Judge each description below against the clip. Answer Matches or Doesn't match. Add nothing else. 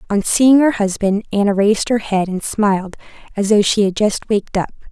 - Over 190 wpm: Matches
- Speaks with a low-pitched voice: Doesn't match